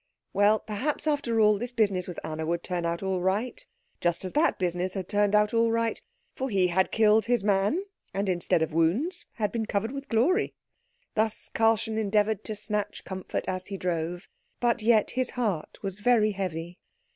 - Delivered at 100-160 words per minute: No, average, 185 wpm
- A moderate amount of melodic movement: Yes, average, 3.7 semitones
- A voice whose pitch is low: No, high, 210 Hz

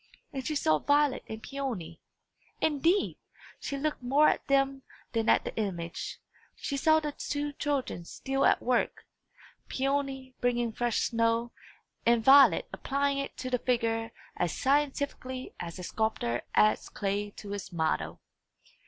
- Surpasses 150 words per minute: No, average, 145 wpm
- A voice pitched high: Yes, very high, 255 Hz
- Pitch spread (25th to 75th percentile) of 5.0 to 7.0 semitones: No, average, 4.2 semitones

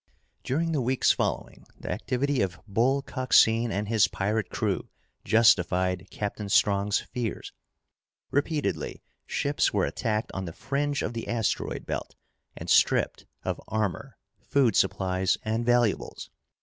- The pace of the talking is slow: Yes, slow, 130 wpm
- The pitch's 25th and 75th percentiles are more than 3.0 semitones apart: Yes, average, 4.5 semitones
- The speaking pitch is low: Yes, low, 110 Hz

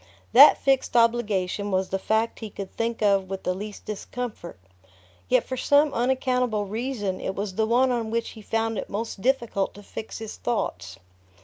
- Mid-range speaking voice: No, high, 220 Hz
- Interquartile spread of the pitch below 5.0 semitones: Yes, average, 3.3 semitones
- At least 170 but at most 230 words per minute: Yes, average, 180 wpm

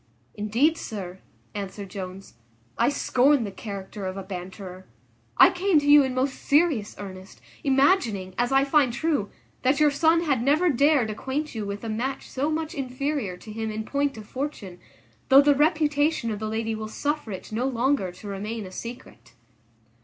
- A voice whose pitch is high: Yes, high, 240 Hz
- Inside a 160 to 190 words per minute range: Yes, average, 175 wpm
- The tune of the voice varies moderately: No, wide, 5.9 semitones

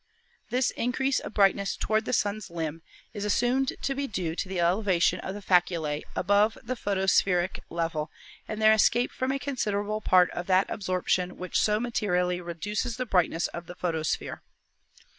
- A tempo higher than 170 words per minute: No, average, 165 wpm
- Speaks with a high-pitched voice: Yes, high, 195 Hz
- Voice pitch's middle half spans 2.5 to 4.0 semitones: Yes, average, 3.6 semitones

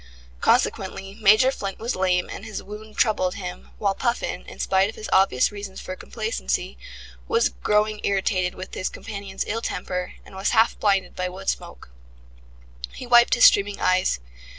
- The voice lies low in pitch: No, high, 200 Hz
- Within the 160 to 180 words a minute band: Yes, average, 165 wpm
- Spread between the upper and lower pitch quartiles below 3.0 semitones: Yes, narrow, 2.6 semitones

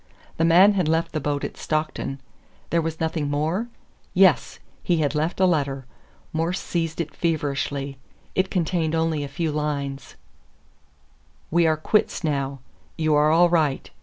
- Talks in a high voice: No, medium, 155 Hz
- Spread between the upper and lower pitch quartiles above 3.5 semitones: No, narrow, 2.5 semitones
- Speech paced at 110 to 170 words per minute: Yes, average, 155 wpm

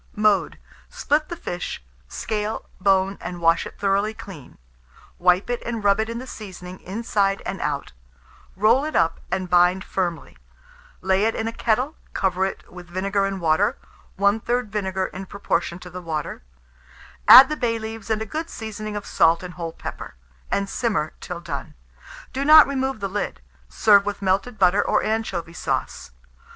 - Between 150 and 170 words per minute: Yes, average, 165 wpm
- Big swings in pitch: No, average, 3.5 semitones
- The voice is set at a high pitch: Yes, high, 200 Hz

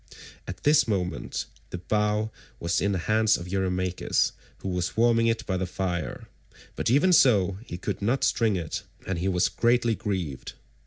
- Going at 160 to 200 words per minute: Yes, average, 170 wpm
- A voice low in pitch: Yes, very low, 95 Hz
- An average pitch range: Yes, average, 4.0 semitones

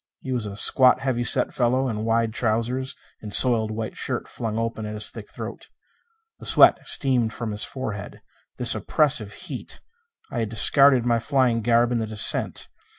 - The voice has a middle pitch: No, low, 115 Hz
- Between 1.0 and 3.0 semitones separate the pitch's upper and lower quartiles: Yes, average, 2.7 semitones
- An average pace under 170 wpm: No, average, 175 wpm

